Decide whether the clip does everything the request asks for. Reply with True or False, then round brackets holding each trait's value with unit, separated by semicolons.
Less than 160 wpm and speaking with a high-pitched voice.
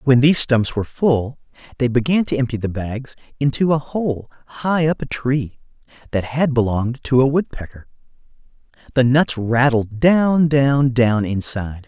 False (145 wpm; 130 Hz)